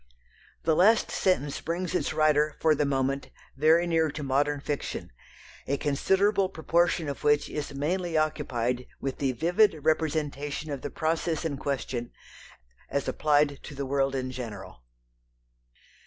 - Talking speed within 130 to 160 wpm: Yes, average, 140 wpm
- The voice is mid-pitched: Yes, medium, 150 Hz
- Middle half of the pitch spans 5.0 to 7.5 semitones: No, average, 2.8 semitones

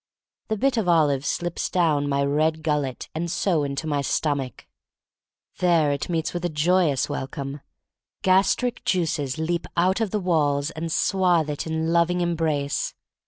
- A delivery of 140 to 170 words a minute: No, average, 190 wpm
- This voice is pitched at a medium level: Yes, medium, 160 Hz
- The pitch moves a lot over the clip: No, average, 3.4 semitones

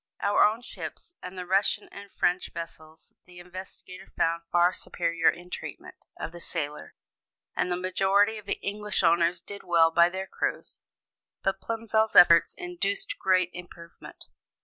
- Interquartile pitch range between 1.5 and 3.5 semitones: Yes, average, 2.9 semitones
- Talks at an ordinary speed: Yes, average, 150 wpm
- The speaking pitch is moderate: Yes, medium, 180 Hz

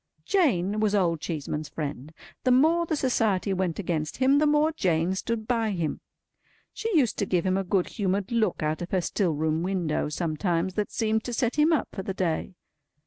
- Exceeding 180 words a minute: Yes, average, 200 wpm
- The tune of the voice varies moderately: No, wide, 5.9 semitones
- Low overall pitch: No, high, 195 Hz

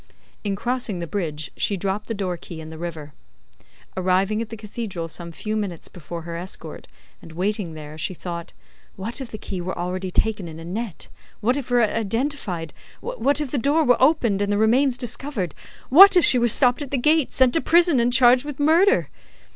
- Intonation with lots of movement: Yes, wide, 6.4 semitones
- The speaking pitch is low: No, high, 215 Hz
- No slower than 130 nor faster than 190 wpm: No, fast, 205 wpm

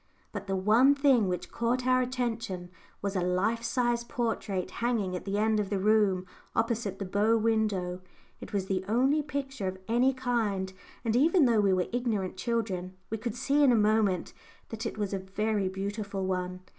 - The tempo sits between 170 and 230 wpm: Yes, average, 185 wpm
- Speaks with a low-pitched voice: No, high, 215 Hz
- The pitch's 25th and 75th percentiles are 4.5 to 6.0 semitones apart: No, average, 3.9 semitones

